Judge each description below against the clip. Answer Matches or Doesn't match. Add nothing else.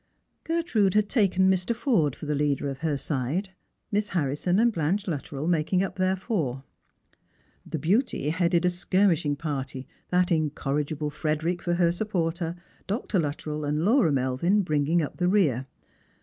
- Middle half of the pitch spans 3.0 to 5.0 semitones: Matches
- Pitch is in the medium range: Matches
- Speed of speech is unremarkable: Matches